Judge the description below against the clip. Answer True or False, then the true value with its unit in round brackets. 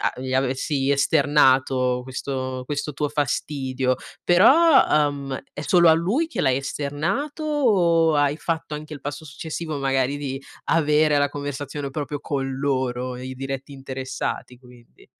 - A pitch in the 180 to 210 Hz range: False (140 Hz)